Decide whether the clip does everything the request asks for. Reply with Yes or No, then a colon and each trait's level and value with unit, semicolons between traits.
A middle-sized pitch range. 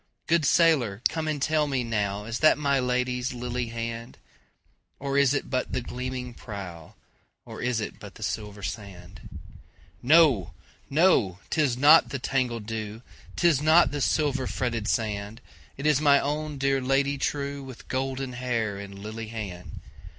Yes: average, 4.1 semitones